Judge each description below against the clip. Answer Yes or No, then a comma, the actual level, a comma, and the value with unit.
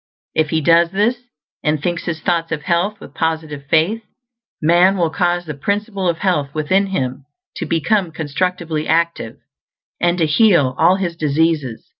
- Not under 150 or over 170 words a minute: Yes, average, 160 wpm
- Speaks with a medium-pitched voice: Yes, medium, 170 Hz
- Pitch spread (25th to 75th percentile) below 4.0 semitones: Yes, average, 3.1 semitones